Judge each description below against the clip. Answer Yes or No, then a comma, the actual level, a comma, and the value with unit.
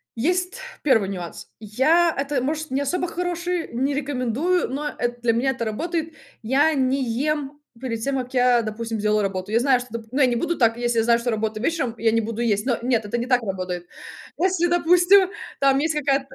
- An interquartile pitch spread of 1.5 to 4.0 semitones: No, average, 5.0 semitones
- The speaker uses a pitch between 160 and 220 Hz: No, very high, 255 Hz